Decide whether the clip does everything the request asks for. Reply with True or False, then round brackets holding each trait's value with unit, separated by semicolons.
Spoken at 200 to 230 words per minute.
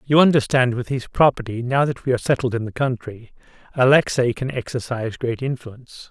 False (175 wpm)